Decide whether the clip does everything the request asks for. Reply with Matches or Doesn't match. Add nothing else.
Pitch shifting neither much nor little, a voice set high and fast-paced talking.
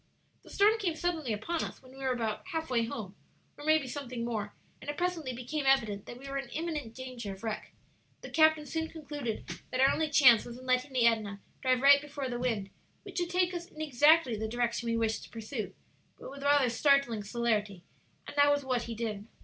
Matches